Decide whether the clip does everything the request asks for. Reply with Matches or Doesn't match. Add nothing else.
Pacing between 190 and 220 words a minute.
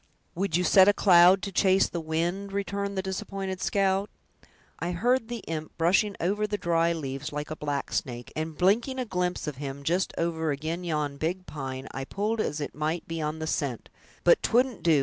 Matches